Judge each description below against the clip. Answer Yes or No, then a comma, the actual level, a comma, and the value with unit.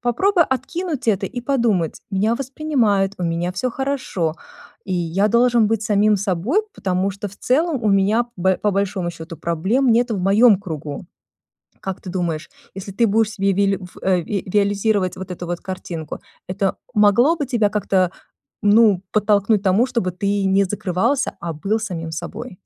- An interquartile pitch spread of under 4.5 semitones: Yes, average, 3.9 semitones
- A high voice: Yes, high, 200 Hz